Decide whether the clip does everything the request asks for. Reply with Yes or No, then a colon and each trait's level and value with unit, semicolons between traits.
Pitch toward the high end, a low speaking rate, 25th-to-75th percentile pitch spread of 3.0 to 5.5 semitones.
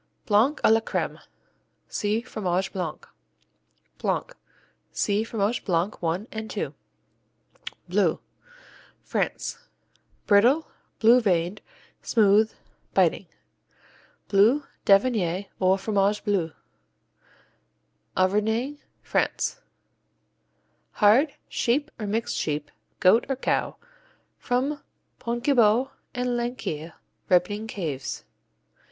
Yes: high, 210 Hz; slow, 85 wpm; average, 4.0 semitones